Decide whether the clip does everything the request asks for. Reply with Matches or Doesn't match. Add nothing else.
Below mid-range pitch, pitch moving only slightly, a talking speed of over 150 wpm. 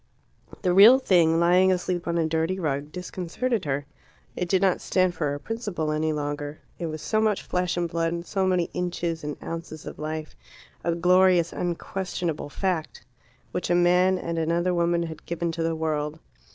Doesn't match